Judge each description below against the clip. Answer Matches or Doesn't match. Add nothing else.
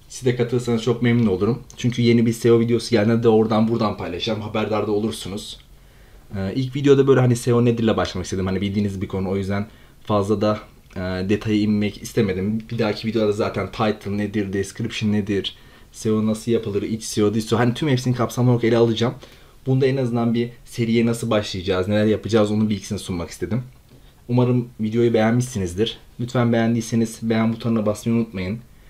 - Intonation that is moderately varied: Doesn't match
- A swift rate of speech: Matches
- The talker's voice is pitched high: Doesn't match